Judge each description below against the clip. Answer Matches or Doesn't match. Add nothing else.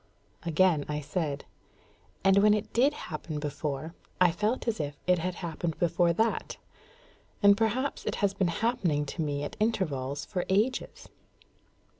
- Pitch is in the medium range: Matches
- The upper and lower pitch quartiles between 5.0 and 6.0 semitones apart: Matches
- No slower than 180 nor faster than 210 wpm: Doesn't match